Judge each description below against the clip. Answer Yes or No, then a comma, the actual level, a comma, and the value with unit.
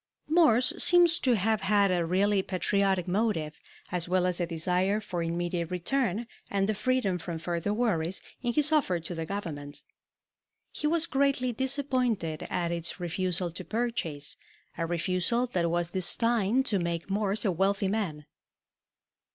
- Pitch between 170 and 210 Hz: Yes, high, 190 Hz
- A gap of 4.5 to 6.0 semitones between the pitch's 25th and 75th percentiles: Yes, average, 5.2 semitones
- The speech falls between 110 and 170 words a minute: Yes, average, 150 wpm